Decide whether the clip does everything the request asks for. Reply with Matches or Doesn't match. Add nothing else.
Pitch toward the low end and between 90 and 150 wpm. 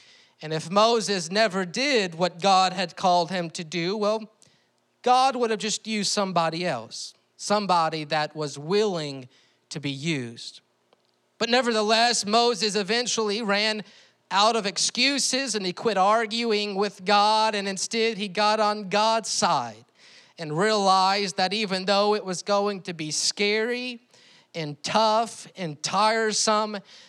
Doesn't match